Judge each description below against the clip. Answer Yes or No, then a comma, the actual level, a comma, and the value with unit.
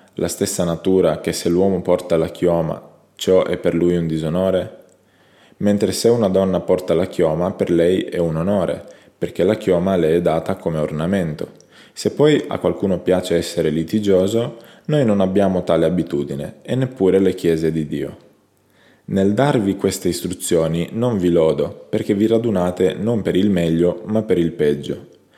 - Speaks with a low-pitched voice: Yes, very low, 90 Hz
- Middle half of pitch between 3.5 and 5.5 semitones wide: No, average, 3.0 semitones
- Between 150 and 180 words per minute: Yes, fast, 170 wpm